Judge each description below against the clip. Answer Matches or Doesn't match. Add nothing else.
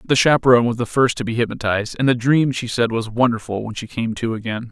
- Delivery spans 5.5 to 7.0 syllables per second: Matches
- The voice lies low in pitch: Matches